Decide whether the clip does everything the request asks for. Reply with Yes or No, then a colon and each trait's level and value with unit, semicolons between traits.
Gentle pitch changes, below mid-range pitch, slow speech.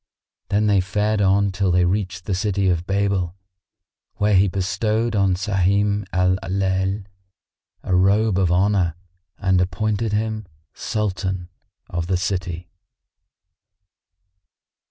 Yes: narrow, 2.1 semitones; very low, 95 Hz; slow, 115 wpm